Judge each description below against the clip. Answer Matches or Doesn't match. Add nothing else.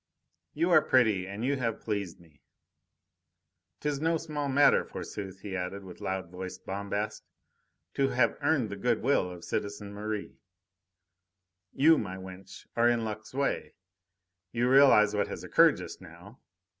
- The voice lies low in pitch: Matches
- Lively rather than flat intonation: Matches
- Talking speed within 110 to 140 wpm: Doesn't match